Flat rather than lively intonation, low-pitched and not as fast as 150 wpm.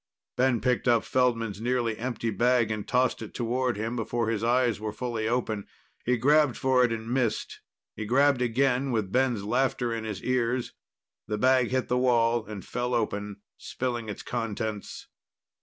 No: narrow, 2.3 semitones; low, 120 Hz; average, 170 wpm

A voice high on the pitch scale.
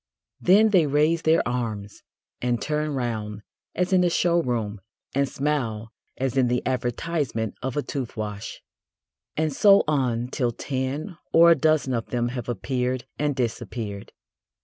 No: low, 130 Hz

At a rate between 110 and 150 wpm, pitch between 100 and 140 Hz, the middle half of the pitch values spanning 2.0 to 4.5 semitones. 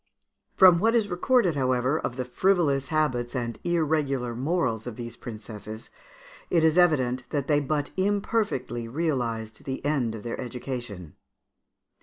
No: average, 140 wpm; low, 135 Hz; average, 5.3 semitones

